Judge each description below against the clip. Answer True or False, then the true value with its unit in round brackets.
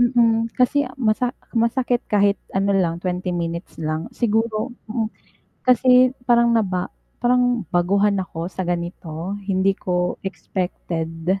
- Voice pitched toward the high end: True (200 Hz)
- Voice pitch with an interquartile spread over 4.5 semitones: True (4.9 semitones)